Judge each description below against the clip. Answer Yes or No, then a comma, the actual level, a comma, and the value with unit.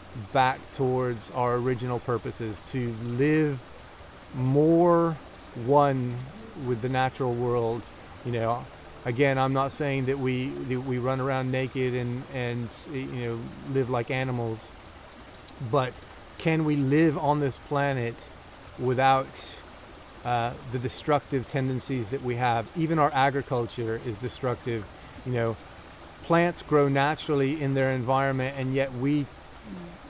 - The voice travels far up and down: No, narrow, 2.5 semitones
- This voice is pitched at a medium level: No, low, 130 Hz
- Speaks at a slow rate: Yes, slow, 130 wpm